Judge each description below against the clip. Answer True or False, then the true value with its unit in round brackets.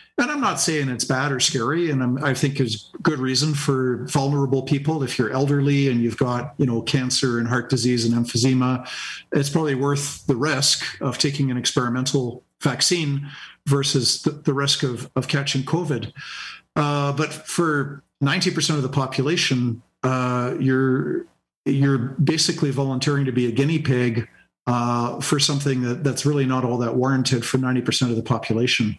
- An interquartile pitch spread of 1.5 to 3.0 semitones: True (2.5 semitones)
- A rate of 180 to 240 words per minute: False (170 wpm)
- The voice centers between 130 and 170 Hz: True (135 Hz)